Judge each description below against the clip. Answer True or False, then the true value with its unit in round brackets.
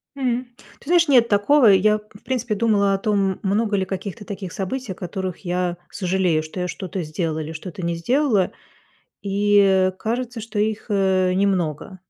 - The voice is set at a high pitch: True (195 Hz)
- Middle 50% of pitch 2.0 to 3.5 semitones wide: True (2.9 semitones)